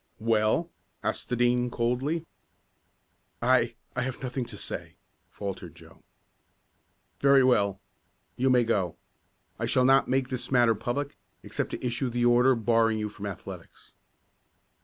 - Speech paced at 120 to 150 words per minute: Yes, slow, 135 wpm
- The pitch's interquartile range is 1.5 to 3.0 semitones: Yes, narrow, 2.6 semitones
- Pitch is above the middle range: No, low, 120 Hz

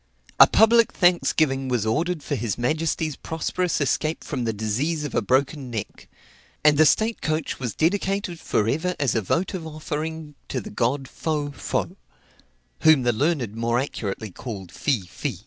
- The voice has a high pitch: No, medium, 145 Hz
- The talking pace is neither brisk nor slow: Yes, average, 165 wpm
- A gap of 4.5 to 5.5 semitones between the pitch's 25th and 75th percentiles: Yes, average, 5.1 semitones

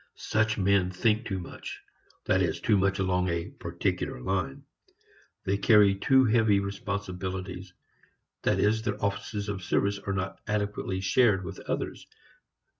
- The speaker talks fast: No, average, 140 wpm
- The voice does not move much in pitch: Yes, narrow, 2.0 semitones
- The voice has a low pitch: Yes, low, 100 Hz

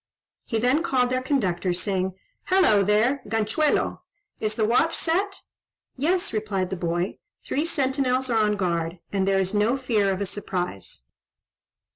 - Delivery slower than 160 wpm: Yes, average, 150 wpm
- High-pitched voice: Yes, high, 215 Hz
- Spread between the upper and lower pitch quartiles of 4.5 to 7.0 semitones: Yes, wide, 5.6 semitones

